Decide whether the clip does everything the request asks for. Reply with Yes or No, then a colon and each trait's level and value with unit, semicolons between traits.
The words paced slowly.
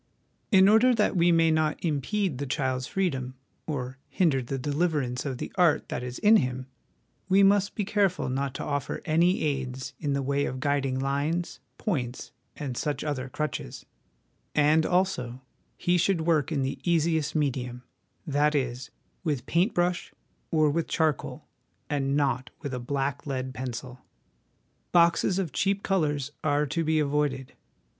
No: average, 155 wpm